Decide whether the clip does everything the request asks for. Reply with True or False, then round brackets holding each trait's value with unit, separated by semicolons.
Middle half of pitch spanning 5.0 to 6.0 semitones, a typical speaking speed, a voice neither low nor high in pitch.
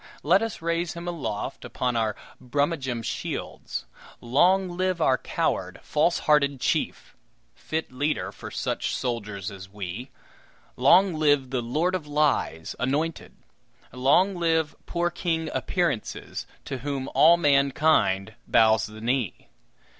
False (5.6 semitones; 125 wpm; 145 Hz)